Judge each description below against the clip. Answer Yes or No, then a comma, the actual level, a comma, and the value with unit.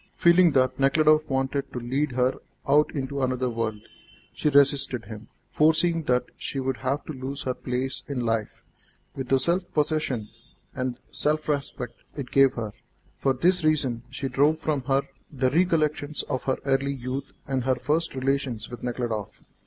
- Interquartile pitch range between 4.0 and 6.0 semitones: No, average, 2.9 semitones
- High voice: No, low, 135 Hz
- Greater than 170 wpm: No, average, 165 wpm